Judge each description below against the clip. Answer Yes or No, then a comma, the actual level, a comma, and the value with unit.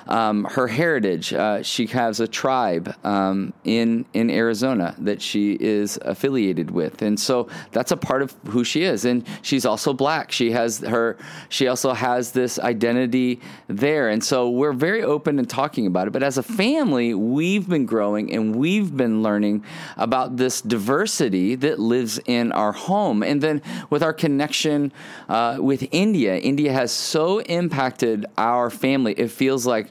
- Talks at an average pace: Yes, average, 170 wpm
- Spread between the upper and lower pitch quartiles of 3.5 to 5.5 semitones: Yes, average, 4.6 semitones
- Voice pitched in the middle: No, low, 125 Hz